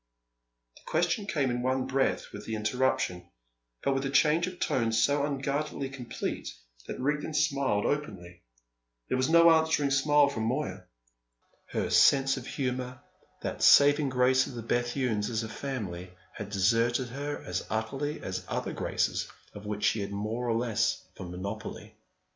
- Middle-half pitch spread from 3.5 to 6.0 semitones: Yes, average, 4.3 semitones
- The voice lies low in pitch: Yes, low, 130 Hz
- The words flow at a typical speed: Yes, average, 160 wpm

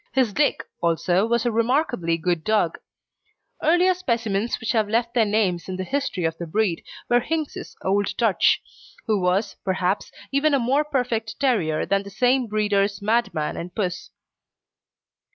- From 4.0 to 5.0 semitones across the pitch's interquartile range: Yes, average, 4.7 semitones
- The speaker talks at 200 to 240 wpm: No, average, 155 wpm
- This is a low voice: No, high, 215 Hz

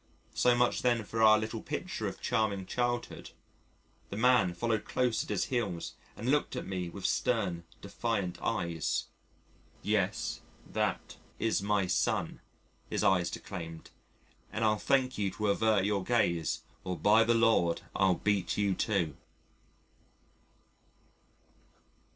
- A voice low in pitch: Yes, low, 105 Hz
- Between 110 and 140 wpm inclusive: Yes, slow, 135 wpm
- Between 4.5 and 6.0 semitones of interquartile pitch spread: No, average, 3.8 semitones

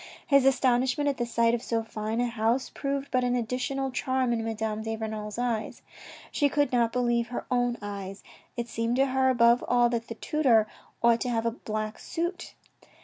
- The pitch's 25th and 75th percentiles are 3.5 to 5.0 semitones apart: No, narrow, 2.4 semitones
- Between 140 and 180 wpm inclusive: No, average, 195 wpm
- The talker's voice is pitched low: No, high, 240 Hz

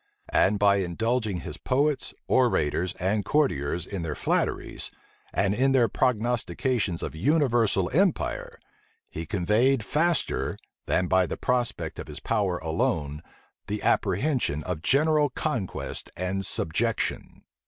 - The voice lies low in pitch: Yes, low, 105 Hz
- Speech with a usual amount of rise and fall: No, wide, 6.5 semitones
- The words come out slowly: Yes, slow, 120 wpm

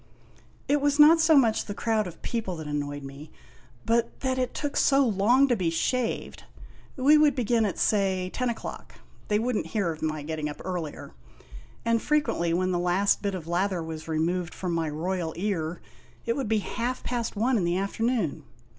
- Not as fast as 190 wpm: No, average, 200 wpm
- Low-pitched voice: No, high, 200 Hz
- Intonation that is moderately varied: No, wide, 6.4 semitones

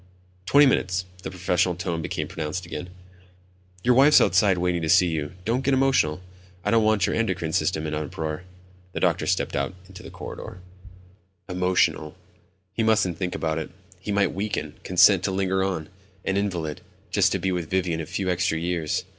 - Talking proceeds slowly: No, average, 180 wpm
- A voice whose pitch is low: Yes, very low, 90 Hz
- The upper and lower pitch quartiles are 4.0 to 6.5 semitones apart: No, average, 3.4 semitones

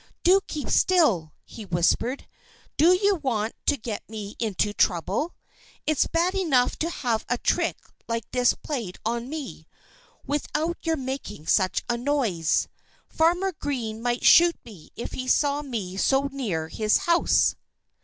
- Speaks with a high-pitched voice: Yes, very high, 250 Hz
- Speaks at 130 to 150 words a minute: Yes, average, 145 wpm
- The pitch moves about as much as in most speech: No, wide, 6.3 semitones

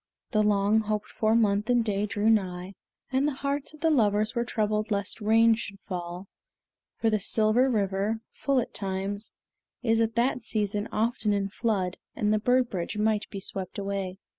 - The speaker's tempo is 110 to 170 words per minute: No, average, 185 wpm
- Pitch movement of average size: No, narrow, 2.3 semitones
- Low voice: No, high, 215 Hz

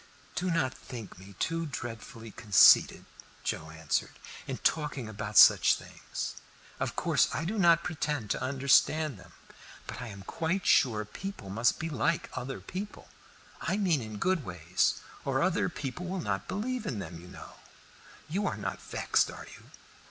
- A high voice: No, low, 135 Hz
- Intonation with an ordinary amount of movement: No, wide, 8.2 semitones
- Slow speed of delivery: No, average, 165 wpm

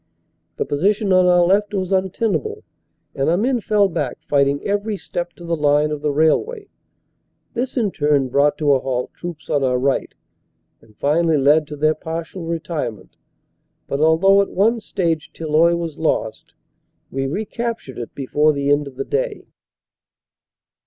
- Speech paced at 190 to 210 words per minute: No, average, 165 wpm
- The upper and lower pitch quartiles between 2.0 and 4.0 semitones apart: No, average, 5.3 semitones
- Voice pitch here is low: No, medium, 160 Hz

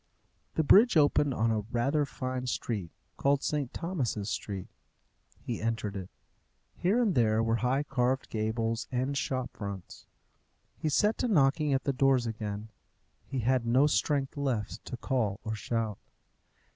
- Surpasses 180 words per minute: No, average, 150 wpm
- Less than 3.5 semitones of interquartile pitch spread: No, average, 4.2 semitones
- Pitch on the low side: Yes, low, 125 Hz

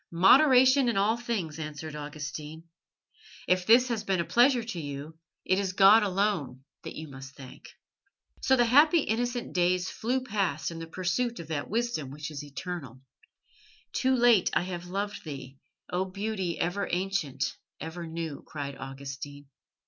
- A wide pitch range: Yes, wide, 6.7 semitones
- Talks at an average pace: Yes, average, 155 wpm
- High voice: No, medium, 180 Hz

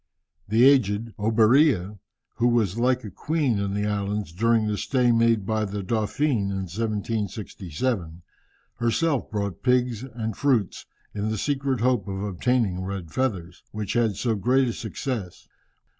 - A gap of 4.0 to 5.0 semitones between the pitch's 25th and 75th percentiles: No, average, 3.6 semitones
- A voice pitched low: Yes, low, 110 Hz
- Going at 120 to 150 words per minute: Yes, average, 145 wpm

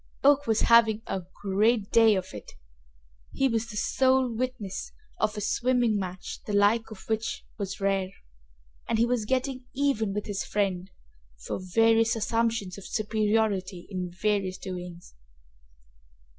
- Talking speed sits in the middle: Yes, average, 145 wpm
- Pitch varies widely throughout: No, average, 3.0 semitones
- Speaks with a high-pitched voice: Yes, high, 215 Hz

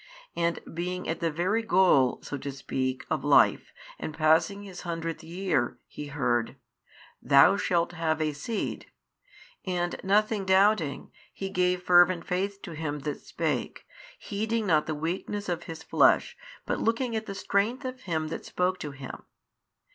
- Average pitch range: Yes, average, 4.0 semitones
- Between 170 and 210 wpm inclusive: No, average, 155 wpm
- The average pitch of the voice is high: No, medium, 175 Hz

